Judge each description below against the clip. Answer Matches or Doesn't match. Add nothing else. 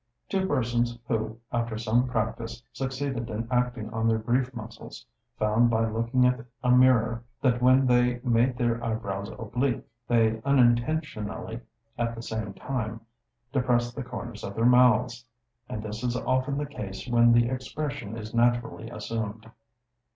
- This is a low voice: Matches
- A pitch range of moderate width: Doesn't match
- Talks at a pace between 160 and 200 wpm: Doesn't match